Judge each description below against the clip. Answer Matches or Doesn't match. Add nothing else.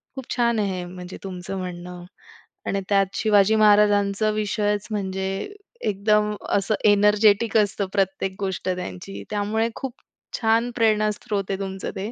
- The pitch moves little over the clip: Matches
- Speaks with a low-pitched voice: Doesn't match